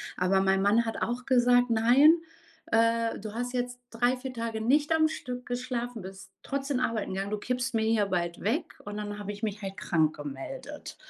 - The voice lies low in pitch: No, high, 230 Hz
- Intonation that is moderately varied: Yes, average, 3.4 semitones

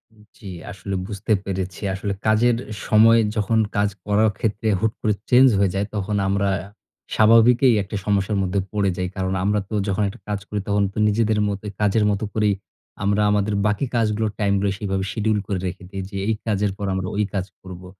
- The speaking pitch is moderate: No, low, 105 Hz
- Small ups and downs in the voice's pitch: Yes, narrow, 1.7 semitones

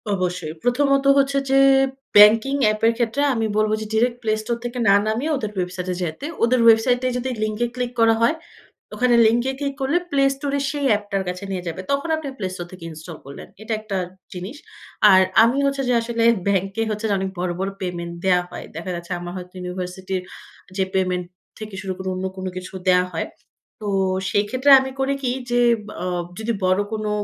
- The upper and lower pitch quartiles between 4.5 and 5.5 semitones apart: Yes, average, 5.1 semitones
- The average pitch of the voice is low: No, high, 215 Hz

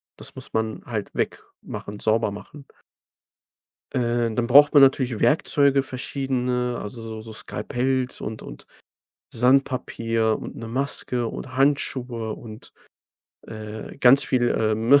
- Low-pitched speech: Yes, low, 120 Hz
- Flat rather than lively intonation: No, average, 3.1 semitones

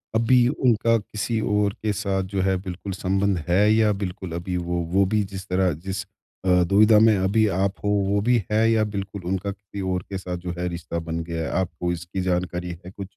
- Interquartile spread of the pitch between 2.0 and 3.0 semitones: Yes, narrow, 2.6 semitones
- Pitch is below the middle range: Yes, very low, 95 Hz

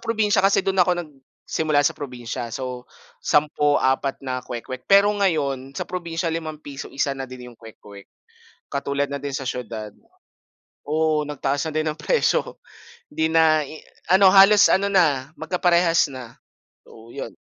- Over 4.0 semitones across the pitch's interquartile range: Yes, average, 4.6 semitones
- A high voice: No, medium, 150 Hz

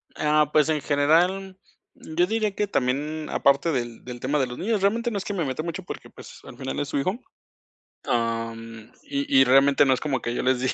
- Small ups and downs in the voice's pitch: No, wide, 5.5 semitones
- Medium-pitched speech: Yes, medium, 145 Hz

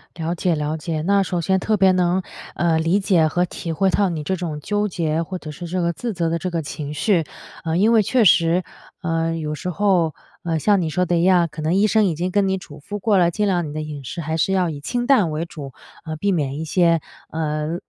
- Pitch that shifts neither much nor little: Yes, average, 3.0 semitones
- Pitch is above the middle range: No, medium, 170 Hz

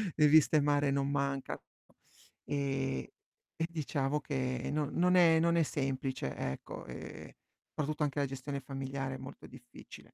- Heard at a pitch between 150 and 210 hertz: No, medium, 140 Hz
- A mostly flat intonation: Yes, narrow, 2.0 semitones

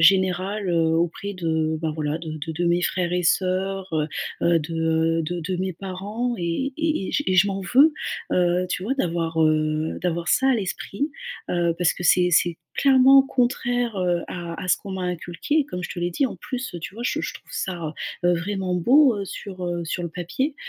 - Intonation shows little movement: No, average, 3.1 semitones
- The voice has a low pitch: No, medium, 180 Hz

